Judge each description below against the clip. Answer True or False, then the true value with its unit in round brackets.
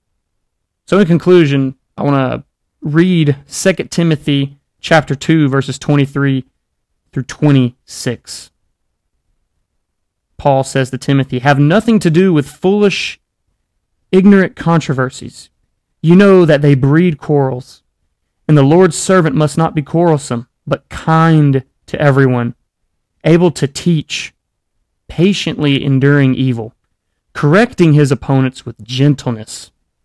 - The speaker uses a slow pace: True (110 wpm)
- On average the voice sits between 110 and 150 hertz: True (140 Hz)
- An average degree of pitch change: True (4.4 semitones)